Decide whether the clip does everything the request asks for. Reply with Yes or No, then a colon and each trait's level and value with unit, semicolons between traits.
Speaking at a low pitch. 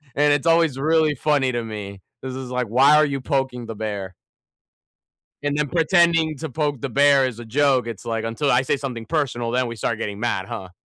Yes: low, 130 Hz